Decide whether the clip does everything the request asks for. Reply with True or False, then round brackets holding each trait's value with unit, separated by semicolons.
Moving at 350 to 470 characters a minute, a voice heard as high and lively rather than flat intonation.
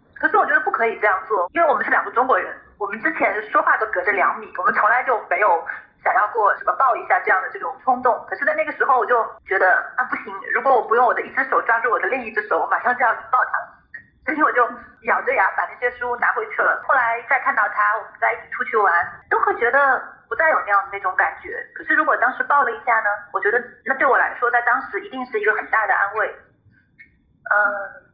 True (365 characters per minute; 245 Hz; 6.1 semitones)